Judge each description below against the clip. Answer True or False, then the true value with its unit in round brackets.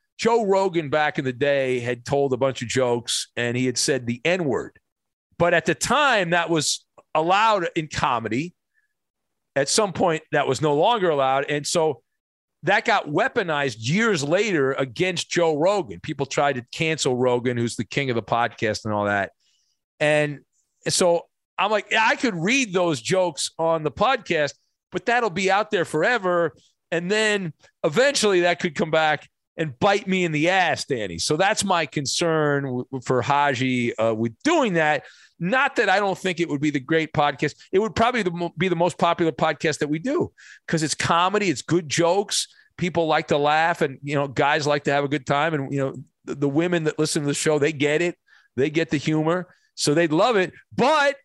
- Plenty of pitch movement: False (4.3 semitones)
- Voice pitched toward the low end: False (160 Hz)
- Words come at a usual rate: True (195 wpm)